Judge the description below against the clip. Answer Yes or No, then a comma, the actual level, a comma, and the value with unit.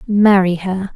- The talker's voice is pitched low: No, high, 190 Hz